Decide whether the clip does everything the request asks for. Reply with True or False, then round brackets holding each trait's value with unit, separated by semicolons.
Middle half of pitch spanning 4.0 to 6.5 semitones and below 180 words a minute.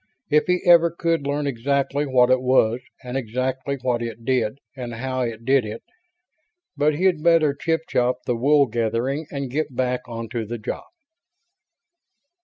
False (3.5 semitones; 160 wpm)